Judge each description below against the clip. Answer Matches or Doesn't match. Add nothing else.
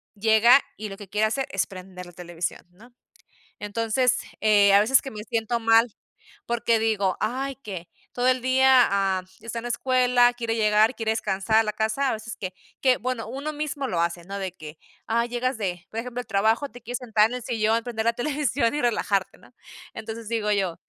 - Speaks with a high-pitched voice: Matches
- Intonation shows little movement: Doesn't match